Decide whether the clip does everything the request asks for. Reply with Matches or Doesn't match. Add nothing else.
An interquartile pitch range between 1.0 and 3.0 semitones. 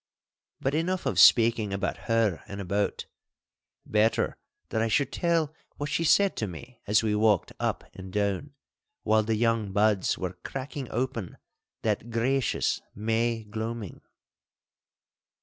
Doesn't match